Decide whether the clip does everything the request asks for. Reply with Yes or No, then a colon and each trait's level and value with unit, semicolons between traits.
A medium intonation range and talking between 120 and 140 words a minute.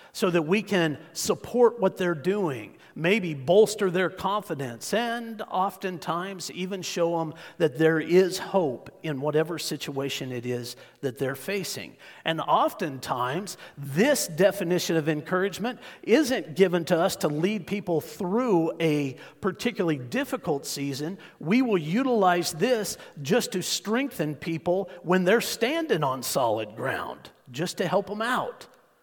Yes: average, 3.9 semitones; slow, 135 wpm